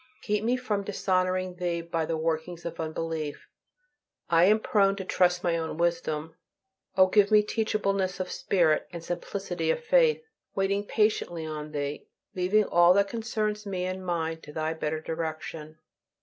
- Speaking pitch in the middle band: Yes, medium, 180 Hz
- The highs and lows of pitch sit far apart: No, average, 3.8 semitones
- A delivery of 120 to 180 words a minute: Yes, average, 160 wpm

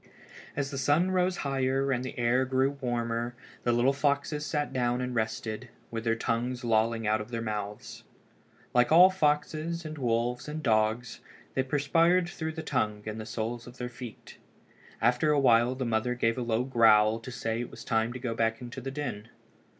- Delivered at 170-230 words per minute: Yes, average, 195 wpm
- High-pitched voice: No, low, 125 Hz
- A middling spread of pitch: Yes, average, 3.3 semitones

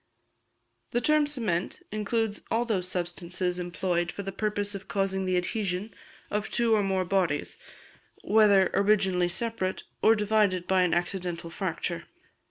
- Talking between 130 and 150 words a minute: Yes, average, 140 wpm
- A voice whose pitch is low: No, high, 190 Hz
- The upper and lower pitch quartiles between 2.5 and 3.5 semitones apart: Yes, average, 3.0 semitones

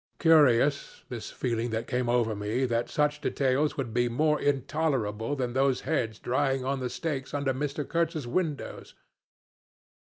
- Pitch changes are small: No, average, 3.5 semitones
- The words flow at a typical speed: Yes, average, 150 wpm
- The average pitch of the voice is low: Yes, low, 130 Hz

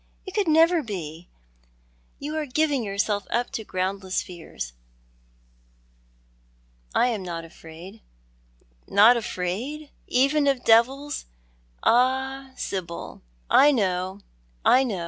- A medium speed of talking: No, slow, 110 wpm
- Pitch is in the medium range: No, high, 225 Hz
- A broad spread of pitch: Yes, wide, 6.8 semitones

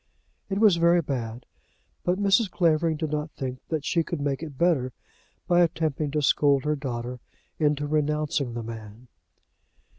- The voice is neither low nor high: Yes, medium, 150 Hz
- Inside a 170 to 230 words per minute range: No, average, 155 wpm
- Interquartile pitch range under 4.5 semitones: Yes, average, 4.1 semitones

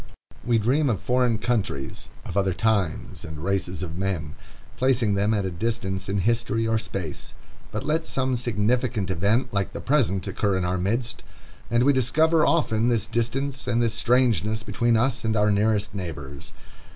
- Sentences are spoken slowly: No, average, 170 wpm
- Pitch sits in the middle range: No, low, 110 Hz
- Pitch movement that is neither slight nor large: Yes, average, 4.0 semitones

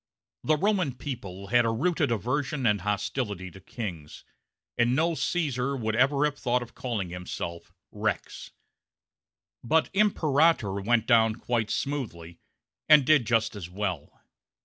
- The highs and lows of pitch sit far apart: Yes, wide, 5.9 semitones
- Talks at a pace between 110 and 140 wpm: Yes, slow, 135 wpm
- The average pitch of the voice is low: Yes, low, 120 Hz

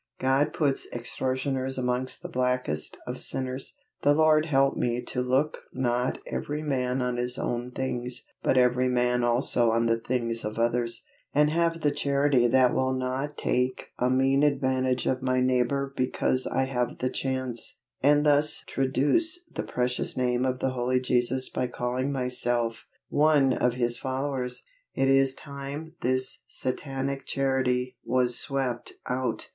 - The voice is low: Yes, low, 130 Hz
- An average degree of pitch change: No, narrow, 1.6 semitones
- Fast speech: No, average, 150 wpm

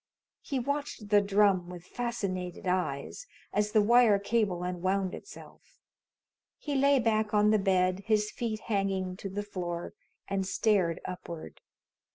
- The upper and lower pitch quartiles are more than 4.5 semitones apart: No, average, 3.0 semitones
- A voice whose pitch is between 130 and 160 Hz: No, high, 200 Hz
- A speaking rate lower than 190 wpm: Yes, average, 140 wpm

